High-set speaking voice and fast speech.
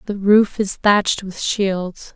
No: high, 200 Hz; average, 165 wpm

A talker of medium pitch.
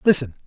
Yes: medium, 145 Hz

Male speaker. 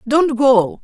No: female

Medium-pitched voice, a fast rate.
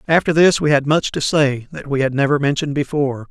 Yes: medium, 145 Hz; fast, 235 wpm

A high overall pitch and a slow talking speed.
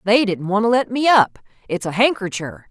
No: high, 210 Hz; fast, 220 wpm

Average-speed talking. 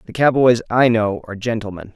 Yes: average, 185 wpm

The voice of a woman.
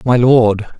No: male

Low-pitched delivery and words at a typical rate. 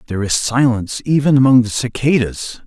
Yes: low, 125 Hz; average, 160 wpm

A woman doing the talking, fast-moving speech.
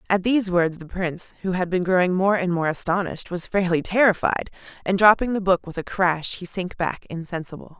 Yes: female; fast, 210 wpm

